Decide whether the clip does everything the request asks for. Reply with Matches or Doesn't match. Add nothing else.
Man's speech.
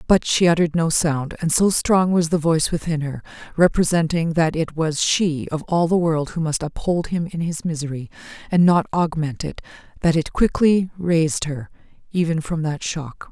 Doesn't match